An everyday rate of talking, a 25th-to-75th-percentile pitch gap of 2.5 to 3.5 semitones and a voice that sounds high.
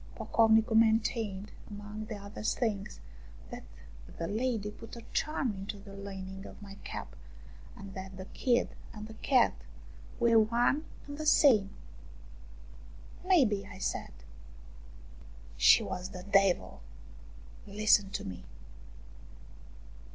No: slow, 120 wpm; average, 2.8 semitones; high, 205 Hz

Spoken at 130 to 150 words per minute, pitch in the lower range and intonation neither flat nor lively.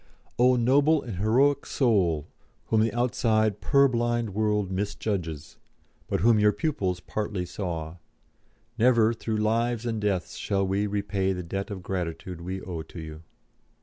Yes: average, 145 wpm; low, 105 Hz; average, 4.1 semitones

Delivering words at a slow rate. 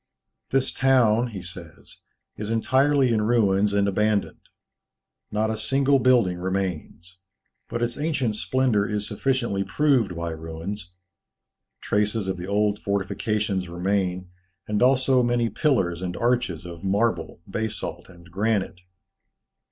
Yes: slow, 125 wpm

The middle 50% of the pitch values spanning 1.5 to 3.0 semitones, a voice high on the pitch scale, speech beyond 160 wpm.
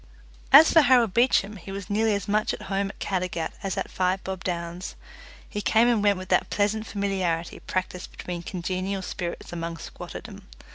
Yes: narrow, 2.4 semitones; high, 195 Hz; average, 180 wpm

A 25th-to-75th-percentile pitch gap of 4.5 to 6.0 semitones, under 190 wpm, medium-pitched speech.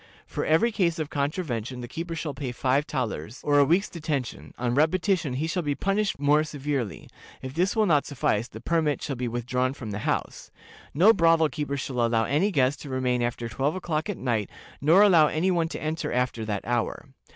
No: average, 4.8 semitones; fast, 205 wpm; medium, 145 Hz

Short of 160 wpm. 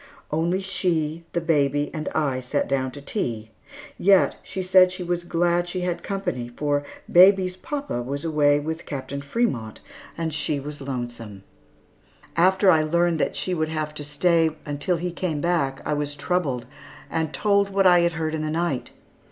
No: average, 175 wpm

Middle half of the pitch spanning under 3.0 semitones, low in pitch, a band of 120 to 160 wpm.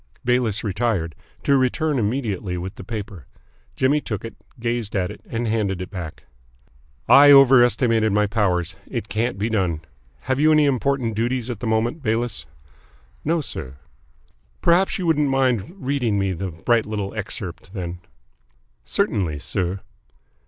No: average, 5.0 semitones; low, 110 Hz; average, 145 wpm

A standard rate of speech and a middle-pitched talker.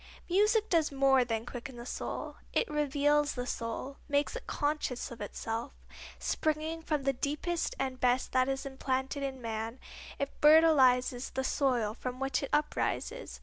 No: average, 155 wpm; very high, 270 Hz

